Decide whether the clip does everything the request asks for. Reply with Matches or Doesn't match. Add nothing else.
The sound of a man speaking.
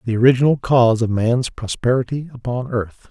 Matches